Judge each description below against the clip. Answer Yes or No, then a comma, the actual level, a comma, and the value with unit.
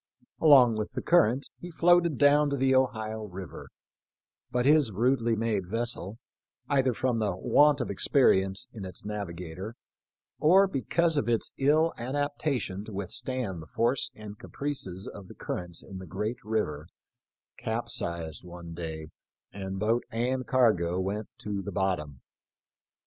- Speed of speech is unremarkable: Yes, average, 145 wpm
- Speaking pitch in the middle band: No, low, 110 Hz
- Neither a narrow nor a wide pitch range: No, wide, 5.7 semitones